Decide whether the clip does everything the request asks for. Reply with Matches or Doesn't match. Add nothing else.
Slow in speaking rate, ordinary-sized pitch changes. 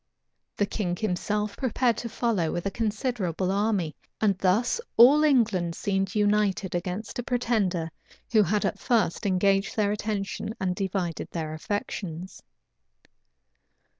Matches